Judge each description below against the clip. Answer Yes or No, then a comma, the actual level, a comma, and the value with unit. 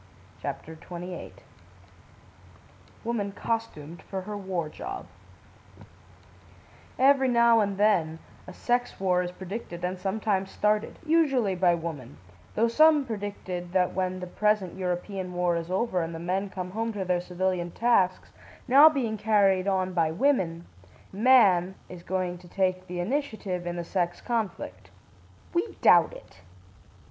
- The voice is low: No, high, 190 Hz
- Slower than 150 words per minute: Yes, average, 140 wpm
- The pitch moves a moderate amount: Yes, average, 3.8 semitones